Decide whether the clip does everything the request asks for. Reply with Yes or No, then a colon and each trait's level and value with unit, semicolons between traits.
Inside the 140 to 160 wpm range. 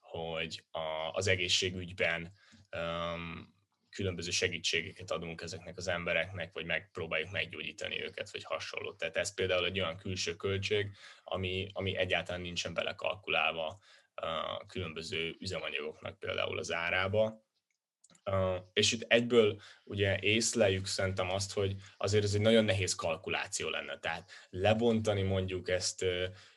No: average, 115 wpm